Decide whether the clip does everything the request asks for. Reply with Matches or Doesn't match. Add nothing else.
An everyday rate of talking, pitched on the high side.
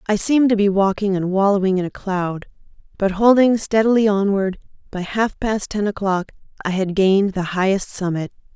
Matches